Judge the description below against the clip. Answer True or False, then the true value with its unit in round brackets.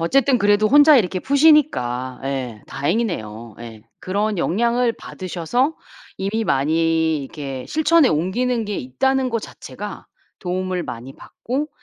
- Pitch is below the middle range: False (185 Hz)